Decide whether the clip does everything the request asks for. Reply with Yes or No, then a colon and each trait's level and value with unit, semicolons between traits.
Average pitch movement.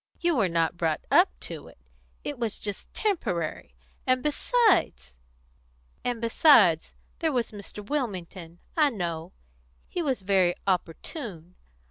No: wide, 8.7 semitones